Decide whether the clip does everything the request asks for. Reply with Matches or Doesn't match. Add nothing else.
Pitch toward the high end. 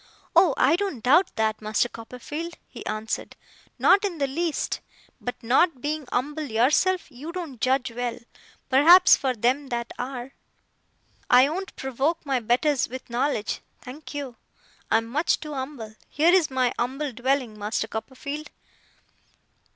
Matches